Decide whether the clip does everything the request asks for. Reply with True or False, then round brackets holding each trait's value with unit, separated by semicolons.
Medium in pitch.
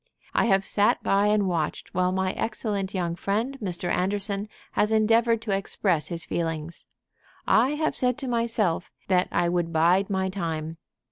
False (195 Hz)